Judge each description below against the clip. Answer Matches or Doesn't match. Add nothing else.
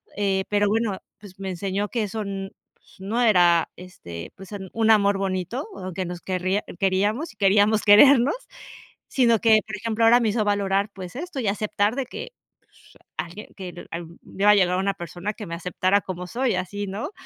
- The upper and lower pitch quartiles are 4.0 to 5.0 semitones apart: Doesn't match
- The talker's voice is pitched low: Doesn't match